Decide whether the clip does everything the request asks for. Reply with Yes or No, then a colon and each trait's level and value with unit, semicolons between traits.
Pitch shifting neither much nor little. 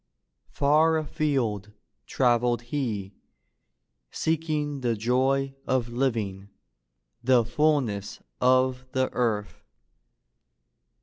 Yes: average, 3.6 semitones